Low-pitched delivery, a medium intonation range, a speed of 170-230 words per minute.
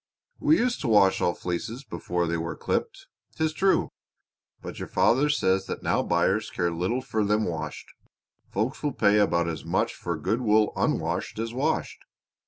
No: low, 105 Hz; wide, 6.4 semitones; average, 175 wpm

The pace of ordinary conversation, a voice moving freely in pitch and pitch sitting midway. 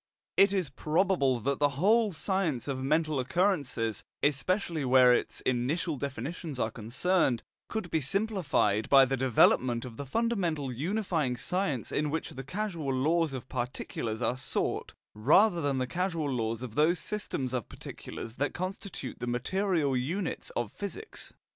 Yes: average, 150 wpm; wide, 6.1 semitones; medium, 145 Hz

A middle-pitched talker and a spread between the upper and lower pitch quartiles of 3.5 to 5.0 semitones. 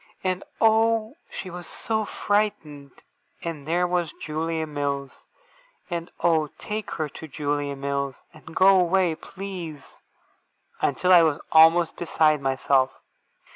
Yes: medium, 165 Hz; average, 4.1 semitones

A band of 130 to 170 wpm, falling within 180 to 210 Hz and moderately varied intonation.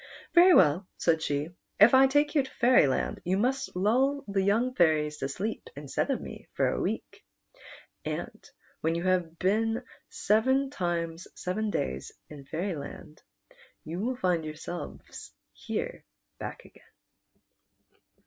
No: average, 140 wpm; medium, 185 Hz; wide, 7.3 semitones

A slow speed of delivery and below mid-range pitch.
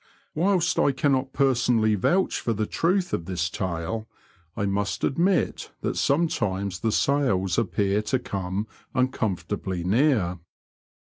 Yes: slow, 125 wpm; low, 110 Hz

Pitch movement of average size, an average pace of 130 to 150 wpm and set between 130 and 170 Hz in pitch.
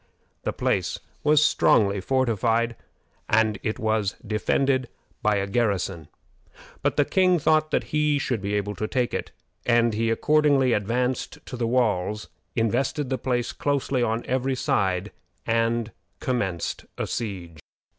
No: average, 3.8 semitones; average, 140 wpm; low, 115 Hz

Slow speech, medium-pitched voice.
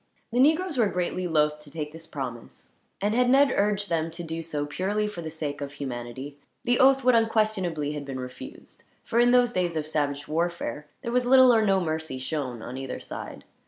No: fast, 205 wpm; medium, 165 Hz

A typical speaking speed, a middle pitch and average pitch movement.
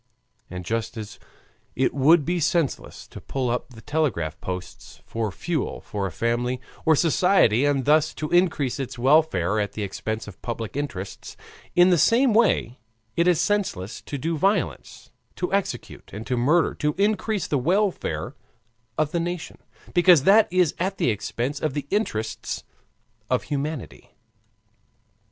No: average, 155 wpm; medium, 145 Hz; wide, 7.2 semitones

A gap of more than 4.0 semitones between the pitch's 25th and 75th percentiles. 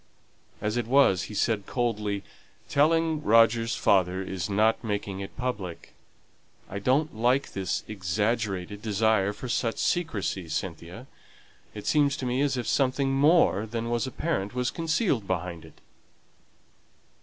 Yes: average, 4.9 semitones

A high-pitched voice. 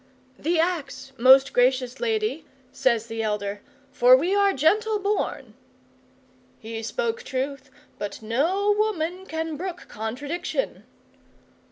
Yes: very high, 290 Hz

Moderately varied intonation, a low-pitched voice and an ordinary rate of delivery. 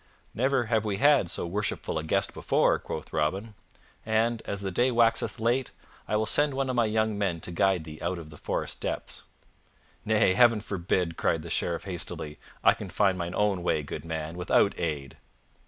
Yes: average, 4.7 semitones; low, 100 Hz; average, 190 wpm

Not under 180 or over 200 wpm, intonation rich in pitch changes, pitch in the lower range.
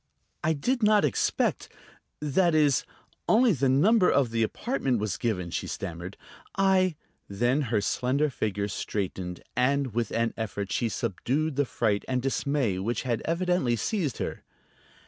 No: average, 150 wpm; wide, 6.2 semitones; low, 130 Hz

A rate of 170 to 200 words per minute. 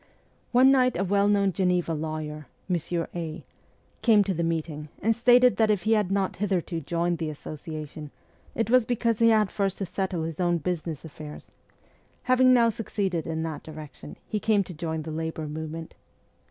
Yes: average, 180 wpm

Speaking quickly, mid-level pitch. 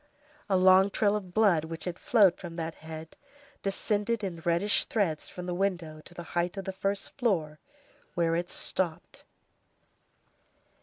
No: average, 155 wpm; medium, 180 Hz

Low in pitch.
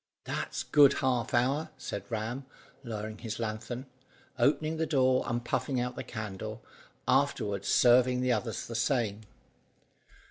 Yes: low, 120 Hz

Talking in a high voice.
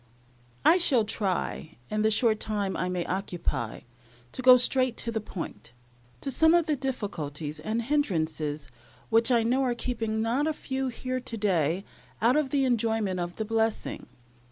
Yes: high, 225 Hz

